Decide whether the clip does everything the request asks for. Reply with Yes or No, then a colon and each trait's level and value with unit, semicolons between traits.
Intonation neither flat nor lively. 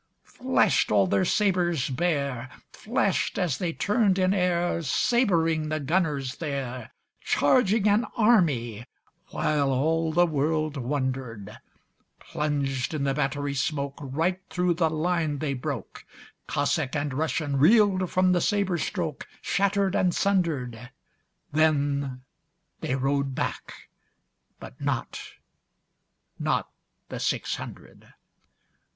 Yes: average, 4.7 semitones